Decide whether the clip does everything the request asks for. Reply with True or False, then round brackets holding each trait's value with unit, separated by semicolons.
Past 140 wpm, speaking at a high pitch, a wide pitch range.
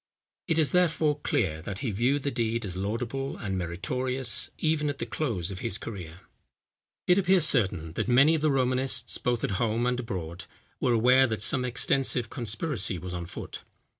False (180 wpm; 120 Hz; 5.9 semitones)